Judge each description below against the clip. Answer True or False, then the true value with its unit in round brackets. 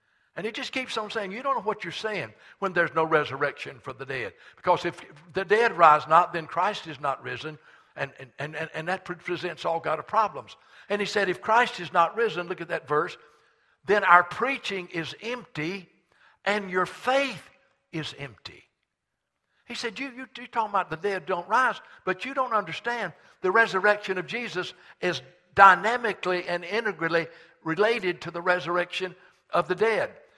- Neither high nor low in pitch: True (180 Hz)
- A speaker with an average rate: True (180 wpm)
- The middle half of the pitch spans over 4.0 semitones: True (4.7 semitones)